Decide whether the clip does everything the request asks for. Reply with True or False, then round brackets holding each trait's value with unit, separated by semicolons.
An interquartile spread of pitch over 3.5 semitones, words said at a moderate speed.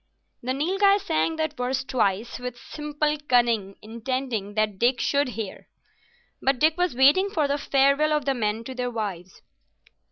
True (4.7 semitones; 160 wpm)